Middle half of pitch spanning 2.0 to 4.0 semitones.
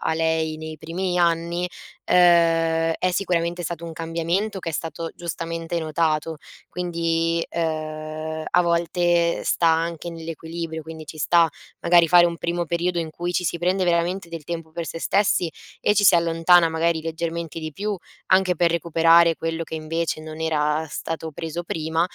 No: narrow, 1.1 semitones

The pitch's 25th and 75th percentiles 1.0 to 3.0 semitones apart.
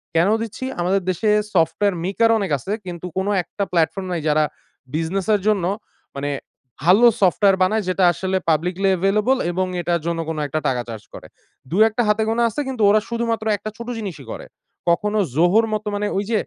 No: average, 3.9 semitones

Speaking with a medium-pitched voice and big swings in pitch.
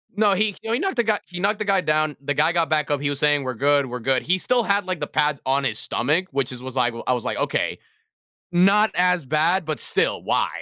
Yes: medium, 155 Hz; wide, 5.7 semitones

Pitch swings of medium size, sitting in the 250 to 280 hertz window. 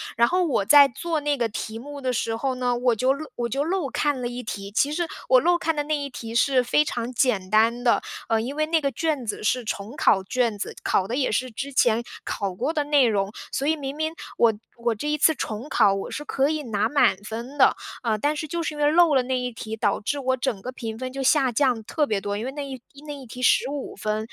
Yes: average, 4.4 semitones; very high, 255 Hz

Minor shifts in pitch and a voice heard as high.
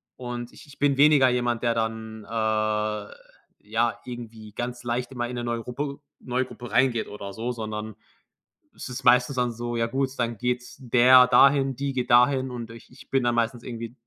No: narrow, 1.9 semitones; low, 120 Hz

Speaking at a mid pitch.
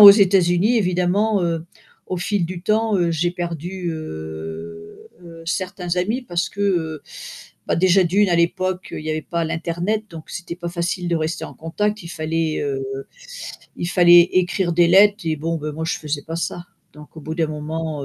Yes: medium, 170 Hz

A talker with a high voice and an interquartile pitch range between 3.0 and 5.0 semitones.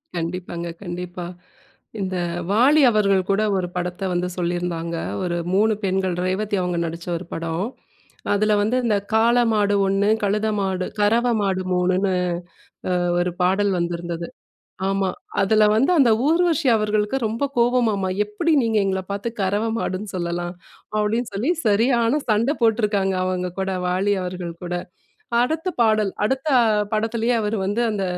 Yes: high, 200 Hz; average, 3.5 semitones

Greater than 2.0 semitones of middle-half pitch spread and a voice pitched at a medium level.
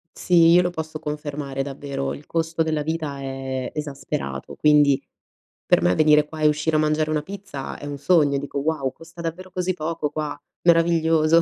Yes: narrow, 2.5 semitones; medium, 150 Hz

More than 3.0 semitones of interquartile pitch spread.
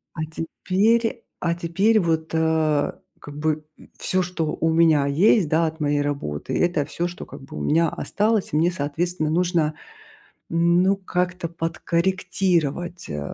No: narrow, 2.6 semitones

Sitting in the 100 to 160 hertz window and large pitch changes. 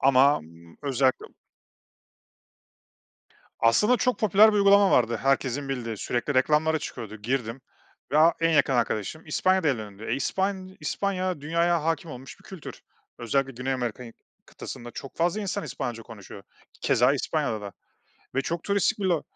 Yes: medium, 140 Hz; wide, 6.6 semitones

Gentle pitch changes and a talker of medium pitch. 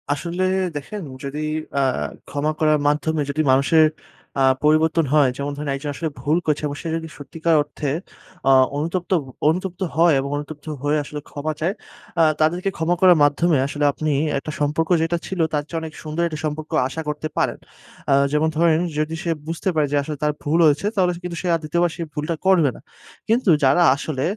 Yes: narrow, 2.3 semitones; medium, 155 Hz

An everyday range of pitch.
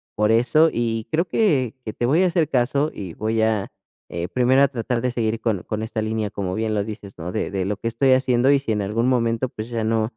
Yes: average, 3.1 semitones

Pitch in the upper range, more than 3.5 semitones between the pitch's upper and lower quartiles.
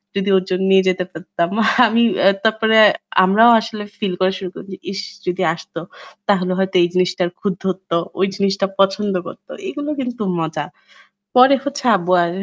No: high, 195 Hz; average, 3.2 semitones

